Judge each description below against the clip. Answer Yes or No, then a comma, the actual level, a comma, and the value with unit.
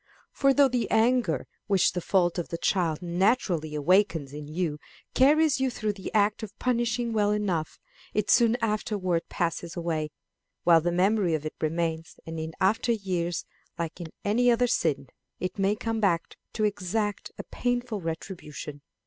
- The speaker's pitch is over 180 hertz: Yes, high, 190 Hz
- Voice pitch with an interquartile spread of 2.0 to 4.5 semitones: No, average, 5.1 semitones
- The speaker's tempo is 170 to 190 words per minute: No, average, 160 wpm